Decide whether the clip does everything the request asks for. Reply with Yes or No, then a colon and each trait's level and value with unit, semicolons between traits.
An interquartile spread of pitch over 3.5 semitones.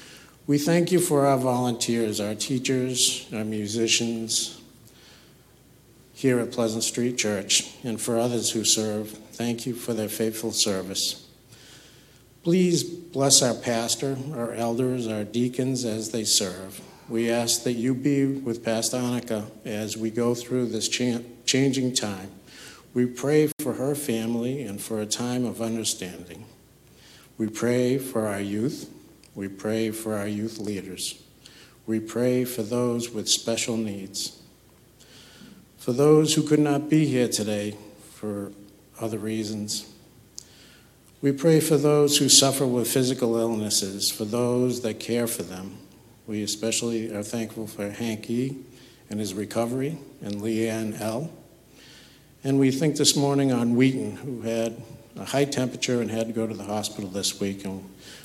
No: average, 3.0 semitones